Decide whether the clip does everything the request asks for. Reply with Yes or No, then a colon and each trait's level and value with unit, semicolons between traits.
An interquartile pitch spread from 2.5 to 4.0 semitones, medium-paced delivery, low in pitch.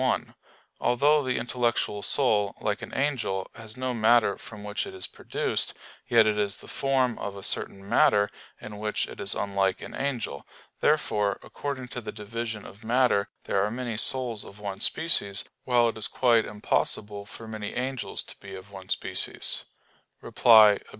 Yes: average, 3.3 semitones; average, 175 wpm; low, 110 Hz